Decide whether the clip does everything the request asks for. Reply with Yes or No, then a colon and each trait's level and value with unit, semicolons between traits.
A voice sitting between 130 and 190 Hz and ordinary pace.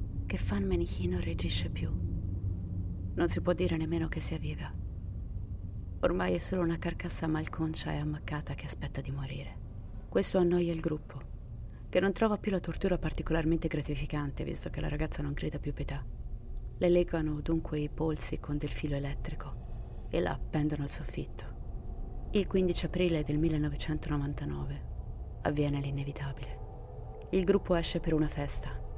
Yes: medium, 140 Hz; average, 150 wpm